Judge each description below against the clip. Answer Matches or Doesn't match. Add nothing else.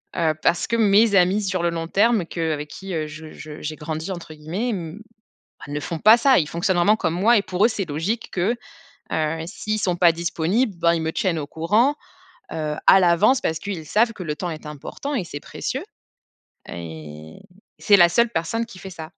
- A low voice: Doesn't match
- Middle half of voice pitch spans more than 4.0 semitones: Matches